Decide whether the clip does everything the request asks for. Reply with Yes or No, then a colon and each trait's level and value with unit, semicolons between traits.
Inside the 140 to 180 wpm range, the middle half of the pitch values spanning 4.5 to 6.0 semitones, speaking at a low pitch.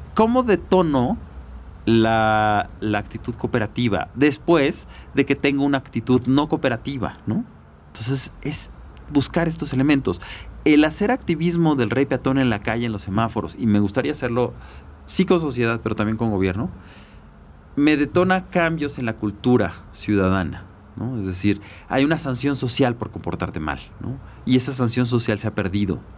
Yes: average, 155 wpm; wide, 5.5 semitones; low, 115 Hz